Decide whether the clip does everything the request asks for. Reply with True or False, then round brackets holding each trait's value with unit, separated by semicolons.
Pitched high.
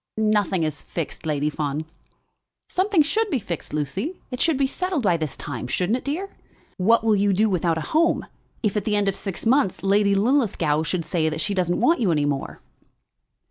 True (195 Hz)